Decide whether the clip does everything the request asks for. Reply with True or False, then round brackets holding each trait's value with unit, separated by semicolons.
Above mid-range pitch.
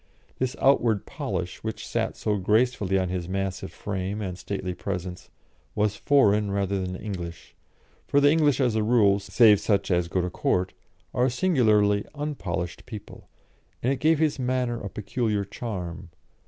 False (105 Hz)